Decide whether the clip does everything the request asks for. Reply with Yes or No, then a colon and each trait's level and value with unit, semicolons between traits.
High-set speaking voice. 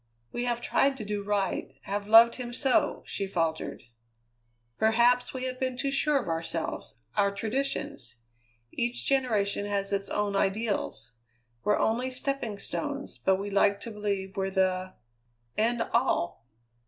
Yes: high, 210 Hz